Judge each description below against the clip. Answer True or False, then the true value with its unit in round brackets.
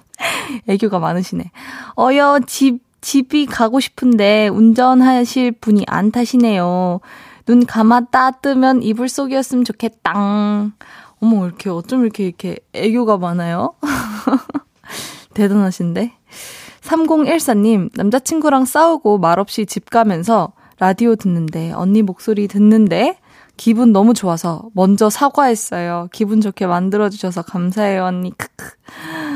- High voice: True (220 Hz)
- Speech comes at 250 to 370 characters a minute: True (270 characters per minute)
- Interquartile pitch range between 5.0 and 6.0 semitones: False (4.6 semitones)